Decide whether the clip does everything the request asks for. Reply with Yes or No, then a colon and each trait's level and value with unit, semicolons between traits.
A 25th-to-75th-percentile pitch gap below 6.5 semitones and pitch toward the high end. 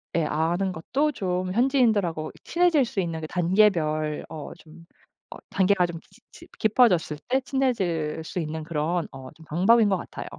No: average, 5.2 semitones; medium, 180 Hz